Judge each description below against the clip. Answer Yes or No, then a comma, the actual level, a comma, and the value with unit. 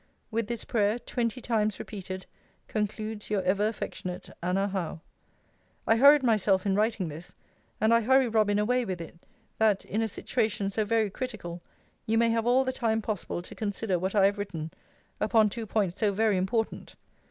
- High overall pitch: Yes, high, 210 Hz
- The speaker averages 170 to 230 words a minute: Yes, average, 175 wpm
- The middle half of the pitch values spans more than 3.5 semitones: No, average, 2.8 semitones